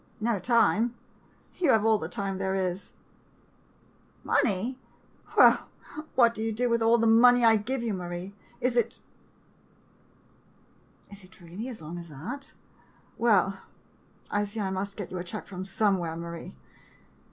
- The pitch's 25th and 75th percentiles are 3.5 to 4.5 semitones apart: Yes, average, 3.9 semitones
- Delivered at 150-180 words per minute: Yes, average, 155 wpm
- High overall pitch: Yes, high, 205 Hz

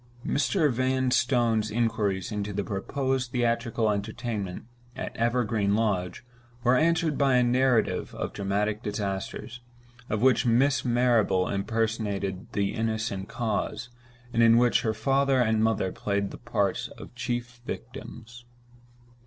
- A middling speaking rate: No, slow, 125 wpm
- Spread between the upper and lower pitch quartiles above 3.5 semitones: No, average, 3.2 semitones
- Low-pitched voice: Yes, low, 115 Hz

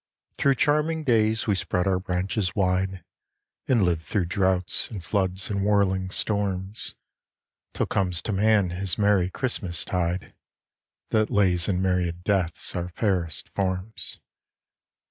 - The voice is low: Yes, very low, 95 Hz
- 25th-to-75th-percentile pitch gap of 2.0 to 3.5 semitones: Yes, narrow, 2.4 semitones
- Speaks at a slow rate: Yes, slow, 130 wpm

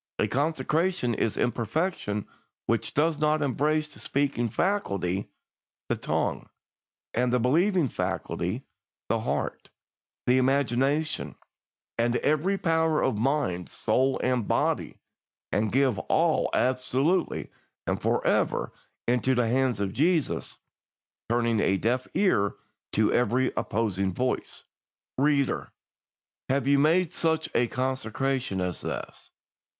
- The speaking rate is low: Yes, slow, 115 wpm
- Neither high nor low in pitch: No, low, 130 Hz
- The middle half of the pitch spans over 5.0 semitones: No, average, 4.5 semitones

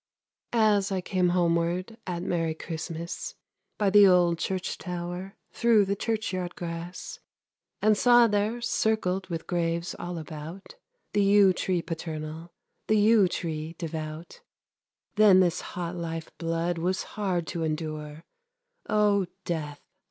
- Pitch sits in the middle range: Yes, medium, 175 Hz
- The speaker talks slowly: Yes, slow, 130 wpm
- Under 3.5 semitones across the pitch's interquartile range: Yes, average, 3.1 semitones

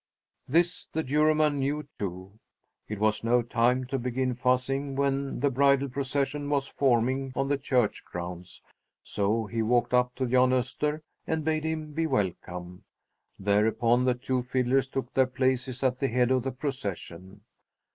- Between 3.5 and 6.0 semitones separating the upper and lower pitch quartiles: No, average, 2.9 semitones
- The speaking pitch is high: No, low, 130 Hz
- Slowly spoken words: No, average, 155 wpm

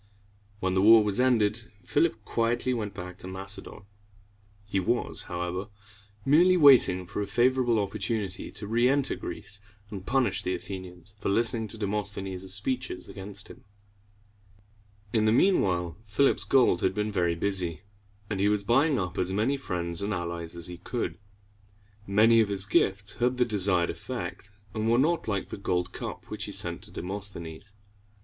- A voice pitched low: Yes, low, 100 Hz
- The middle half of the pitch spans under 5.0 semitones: Yes, average, 3.9 semitones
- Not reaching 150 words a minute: No, average, 165 wpm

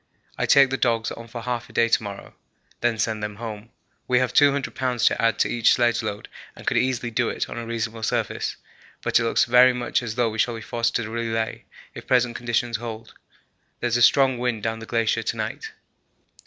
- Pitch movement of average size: No, narrow, 1.5 semitones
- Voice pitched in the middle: No, low, 115 Hz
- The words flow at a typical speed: No, fast, 220 wpm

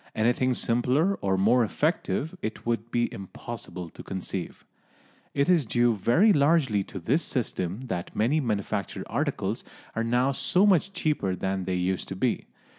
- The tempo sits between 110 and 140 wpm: No, average, 155 wpm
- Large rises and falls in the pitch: Yes, wide, 6.6 semitones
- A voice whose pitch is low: Yes, low, 120 Hz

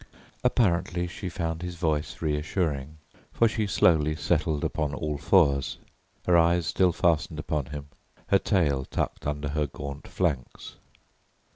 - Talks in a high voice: No, very low, 80 Hz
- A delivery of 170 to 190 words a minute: No, slow, 135 wpm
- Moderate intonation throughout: Yes, average, 3.1 semitones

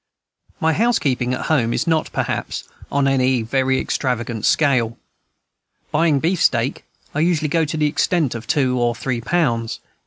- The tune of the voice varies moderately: Yes, average, 4.7 semitones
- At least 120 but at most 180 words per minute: Yes, average, 150 wpm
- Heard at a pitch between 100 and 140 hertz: Yes, low, 135 Hz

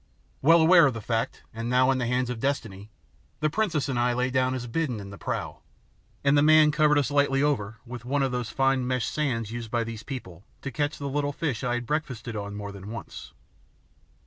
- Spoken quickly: Yes, fast, 225 wpm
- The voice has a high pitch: No, low, 130 Hz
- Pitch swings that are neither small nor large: Yes, average, 3.8 semitones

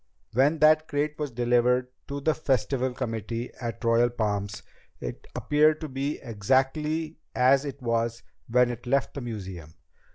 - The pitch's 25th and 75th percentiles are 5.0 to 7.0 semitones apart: No, average, 3.7 semitones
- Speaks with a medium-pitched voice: No, low, 125 Hz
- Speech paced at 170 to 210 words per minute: No, average, 155 wpm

